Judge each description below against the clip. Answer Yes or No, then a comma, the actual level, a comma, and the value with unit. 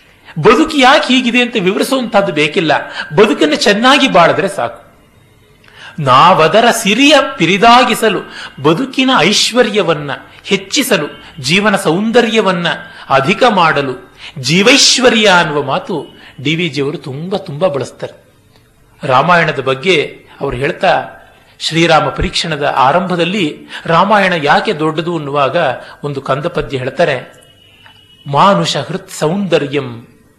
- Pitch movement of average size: No, wide, 6.9 semitones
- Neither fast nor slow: Yes, average, 90 wpm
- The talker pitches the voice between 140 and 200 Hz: Yes, medium, 185 Hz